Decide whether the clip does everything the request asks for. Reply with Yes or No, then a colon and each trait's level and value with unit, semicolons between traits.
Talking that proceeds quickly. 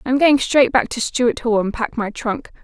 Yes: fast, 250 wpm